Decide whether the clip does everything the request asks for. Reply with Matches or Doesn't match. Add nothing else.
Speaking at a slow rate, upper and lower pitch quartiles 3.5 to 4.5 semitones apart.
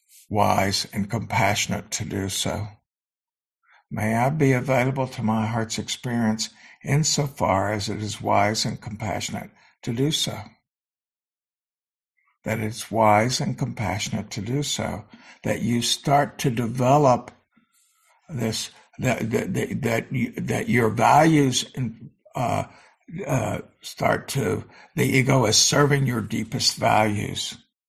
Matches